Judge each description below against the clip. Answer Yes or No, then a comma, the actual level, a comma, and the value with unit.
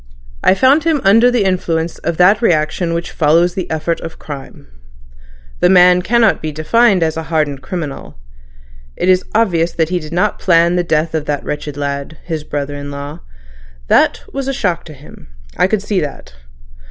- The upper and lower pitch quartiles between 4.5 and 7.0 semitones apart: No, average, 3.7 semitones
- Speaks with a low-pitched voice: No, medium, 170 Hz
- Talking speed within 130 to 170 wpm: No, average, 180 wpm